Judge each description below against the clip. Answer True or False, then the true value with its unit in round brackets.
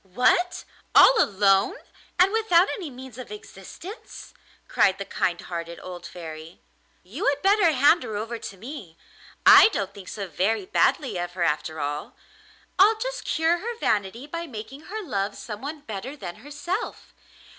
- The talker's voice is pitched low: False (230 Hz)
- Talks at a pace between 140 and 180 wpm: True (155 wpm)